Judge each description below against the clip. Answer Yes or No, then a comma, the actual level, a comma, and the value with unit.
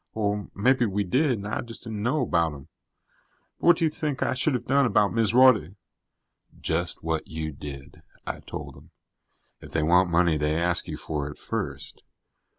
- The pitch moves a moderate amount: No, wide, 7.3 semitones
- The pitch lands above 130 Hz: No, low, 100 Hz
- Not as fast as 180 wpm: No, average, 185 wpm